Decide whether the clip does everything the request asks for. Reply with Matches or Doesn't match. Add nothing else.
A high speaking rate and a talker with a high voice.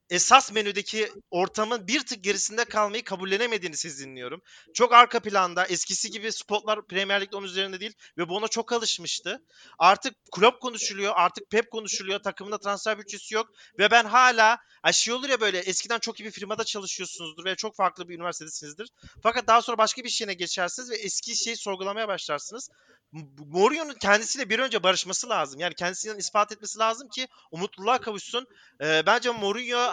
Matches